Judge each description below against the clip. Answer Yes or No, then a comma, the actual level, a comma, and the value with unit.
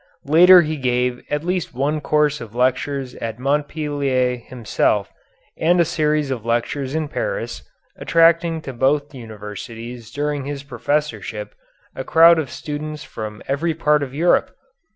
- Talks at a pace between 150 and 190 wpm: No, average, 140 wpm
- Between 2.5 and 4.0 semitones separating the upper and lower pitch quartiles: Yes, average, 3.7 semitones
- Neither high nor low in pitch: Yes, medium, 145 Hz